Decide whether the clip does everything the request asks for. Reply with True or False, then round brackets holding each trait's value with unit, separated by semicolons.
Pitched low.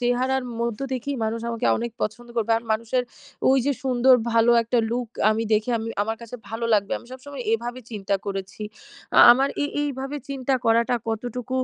False (240 Hz)